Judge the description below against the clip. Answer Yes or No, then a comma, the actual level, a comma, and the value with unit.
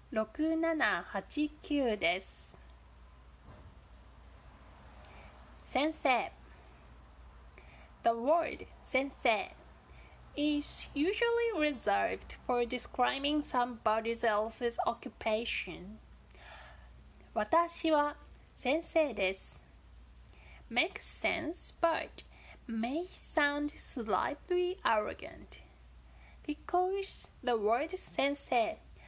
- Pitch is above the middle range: Yes, high, 230 Hz